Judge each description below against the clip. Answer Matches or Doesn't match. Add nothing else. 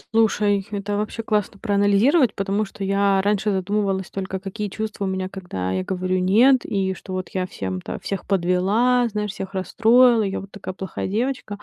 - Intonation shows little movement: Matches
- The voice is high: Matches